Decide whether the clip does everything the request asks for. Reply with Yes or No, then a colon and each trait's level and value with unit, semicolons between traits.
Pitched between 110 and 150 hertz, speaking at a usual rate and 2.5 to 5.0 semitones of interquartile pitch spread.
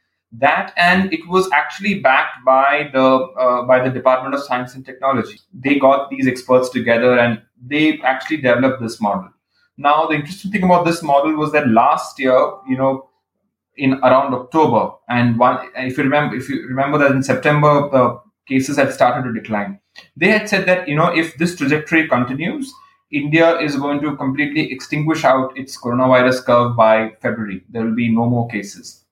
Yes: low, 135 Hz; average, 180 wpm; average, 3.5 semitones